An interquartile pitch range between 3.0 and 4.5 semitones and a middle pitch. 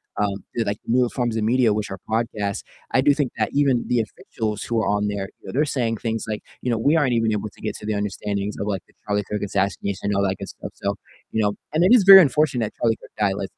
No: average, 3.3 semitones; low, 110 Hz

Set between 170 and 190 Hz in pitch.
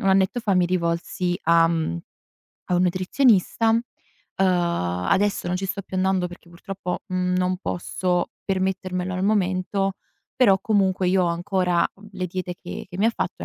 Yes: medium, 185 Hz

